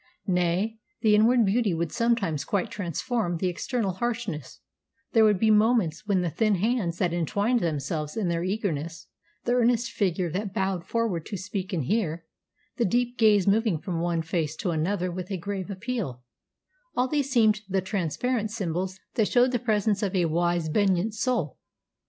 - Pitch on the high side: Yes, high, 195 Hz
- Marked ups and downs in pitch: No, average, 4.6 semitones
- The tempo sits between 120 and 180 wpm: Yes, average, 170 wpm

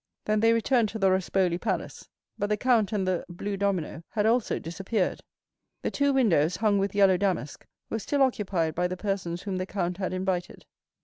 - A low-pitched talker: No, high, 195 Hz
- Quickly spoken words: No, average, 190 wpm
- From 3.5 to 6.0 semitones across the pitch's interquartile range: No, average, 2.9 semitones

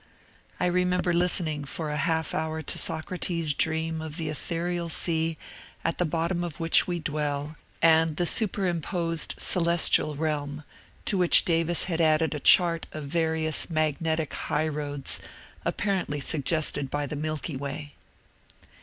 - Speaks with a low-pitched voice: No, medium, 160 Hz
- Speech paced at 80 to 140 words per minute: Yes, slow, 135 wpm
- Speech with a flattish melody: Yes, narrow, 2.1 semitones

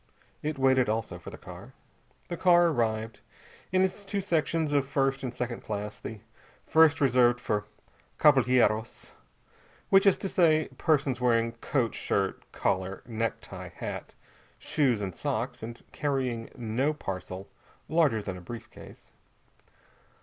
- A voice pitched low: Yes, low, 125 Hz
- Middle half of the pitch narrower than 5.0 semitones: No, average, 5.3 semitones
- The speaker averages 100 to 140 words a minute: Yes, slow, 135 wpm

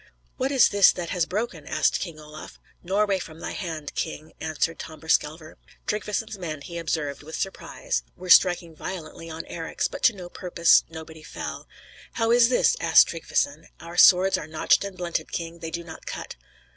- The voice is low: No, medium, 170 Hz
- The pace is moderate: Yes, average, 175 wpm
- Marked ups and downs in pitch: No, average, 3.1 semitones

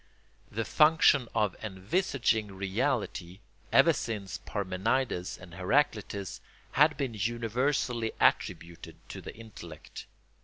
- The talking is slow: Yes, slow, 100 wpm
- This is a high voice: No, low, 110 Hz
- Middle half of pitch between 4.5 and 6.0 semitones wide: Yes, average, 5.2 semitones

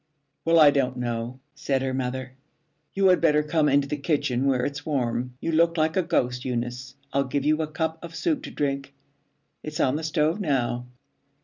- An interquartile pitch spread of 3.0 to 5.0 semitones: Yes, average, 3.7 semitones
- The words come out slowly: No, average, 195 wpm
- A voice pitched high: No, medium, 140 Hz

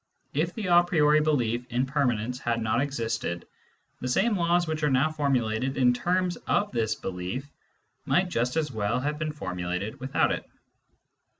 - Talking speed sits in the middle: Yes, average, 165 wpm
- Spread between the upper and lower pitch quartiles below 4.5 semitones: No, average, 5.3 semitones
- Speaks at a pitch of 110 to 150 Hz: Yes, low, 135 Hz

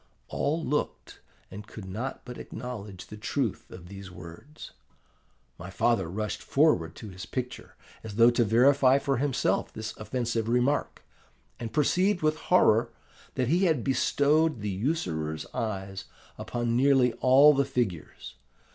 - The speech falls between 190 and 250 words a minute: No, average, 140 wpm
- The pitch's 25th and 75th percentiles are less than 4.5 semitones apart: No, average, 5.2 semitones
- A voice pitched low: Yes, low, 120 Hz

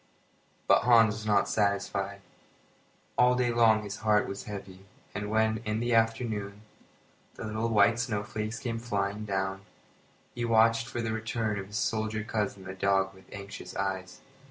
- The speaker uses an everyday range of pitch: No, narrow, 2.1 semitones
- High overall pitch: No, low, 110 Hz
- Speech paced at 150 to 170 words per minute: Yes, average, 160 wpm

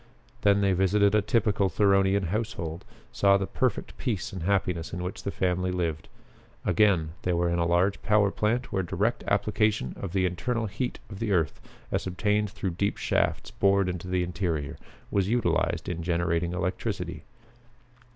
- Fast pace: No, average, 165 wpm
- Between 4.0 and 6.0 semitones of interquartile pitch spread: No, average, 2.8 semitones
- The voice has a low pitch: Yes, very low, 95 Hz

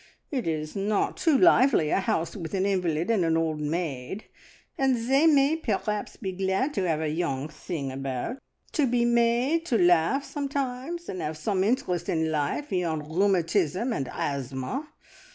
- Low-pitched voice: No, high, 190 Hz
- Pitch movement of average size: No, wide, 7.8 semitones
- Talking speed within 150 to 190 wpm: Yes, average, 165 wpm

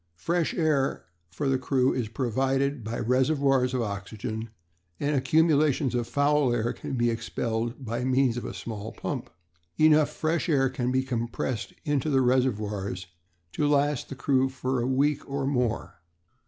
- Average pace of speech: Yes, average, 155 wpm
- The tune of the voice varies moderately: Yes, average, 3.1 semitones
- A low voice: Yes, low, 130 Hz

